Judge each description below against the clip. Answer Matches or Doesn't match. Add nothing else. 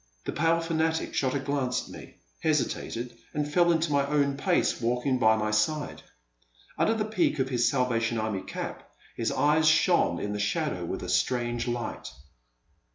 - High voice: Doesn't match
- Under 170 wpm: Doesn't match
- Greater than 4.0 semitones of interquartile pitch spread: Matches